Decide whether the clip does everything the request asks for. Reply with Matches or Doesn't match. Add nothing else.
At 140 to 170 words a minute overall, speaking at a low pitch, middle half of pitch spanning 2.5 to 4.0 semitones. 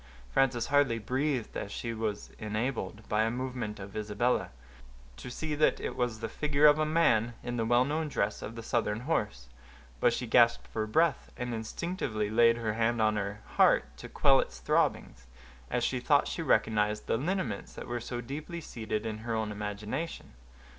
Doesn't match